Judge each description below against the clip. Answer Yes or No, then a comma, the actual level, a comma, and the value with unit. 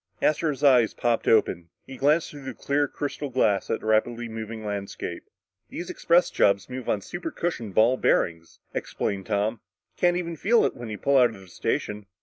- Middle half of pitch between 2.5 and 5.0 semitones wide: No, wide, 5.5 semitones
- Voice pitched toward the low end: Yes, low, 120 Hz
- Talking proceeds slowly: No, average, 185 wpm